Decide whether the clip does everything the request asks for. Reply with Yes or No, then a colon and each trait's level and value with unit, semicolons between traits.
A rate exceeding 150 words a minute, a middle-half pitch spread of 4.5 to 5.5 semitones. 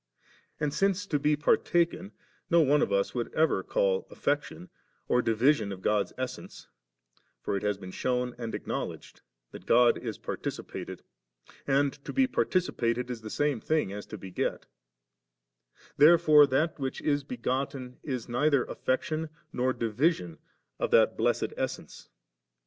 No: average, 145 wpm; average, 4.9 semitones